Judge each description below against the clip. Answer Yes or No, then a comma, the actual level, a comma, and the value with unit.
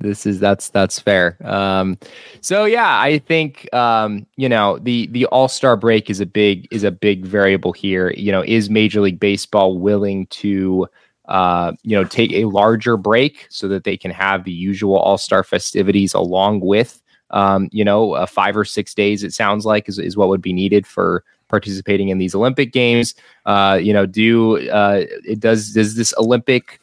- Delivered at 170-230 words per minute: Yes, average, 190 wpm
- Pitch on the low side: Yes, low, 100 Hz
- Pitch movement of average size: No, narrow, 2.3 semitones